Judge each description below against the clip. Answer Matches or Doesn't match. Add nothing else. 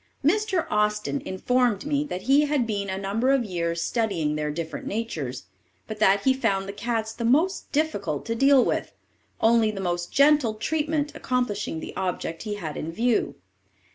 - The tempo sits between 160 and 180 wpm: Matches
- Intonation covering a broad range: Matches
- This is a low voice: Doesn't match